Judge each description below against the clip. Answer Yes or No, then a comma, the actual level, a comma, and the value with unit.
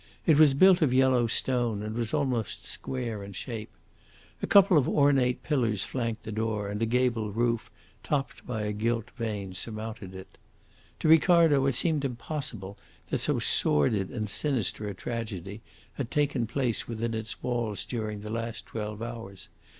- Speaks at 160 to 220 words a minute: Yes, average, 165 wpm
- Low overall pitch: Yes, low, 115 Hz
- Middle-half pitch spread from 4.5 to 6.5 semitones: No, average, 3.6 semitones